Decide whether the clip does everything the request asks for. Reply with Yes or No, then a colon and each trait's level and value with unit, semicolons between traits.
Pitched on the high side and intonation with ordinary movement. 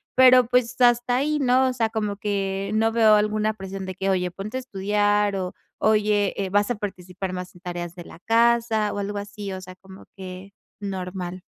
Yes: high, 205 Hz; average, 3.0 semitones